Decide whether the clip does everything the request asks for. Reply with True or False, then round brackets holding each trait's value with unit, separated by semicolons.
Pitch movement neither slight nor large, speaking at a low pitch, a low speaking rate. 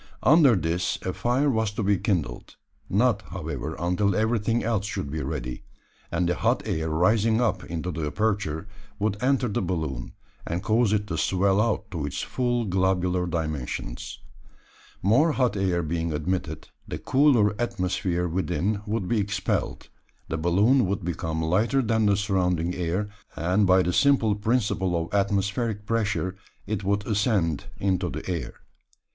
False (4.0 semitones; 95 Hz; 155 wpm)